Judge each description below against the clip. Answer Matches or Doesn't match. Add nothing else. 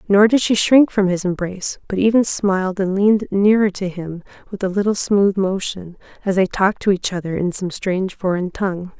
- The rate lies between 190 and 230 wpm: Matches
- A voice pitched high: Matches